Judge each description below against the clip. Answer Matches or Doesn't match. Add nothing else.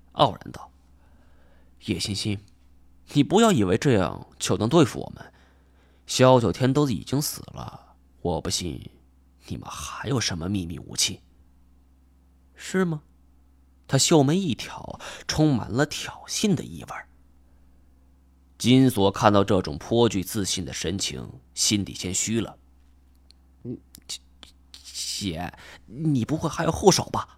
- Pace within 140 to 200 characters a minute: Matches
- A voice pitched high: Doesn't match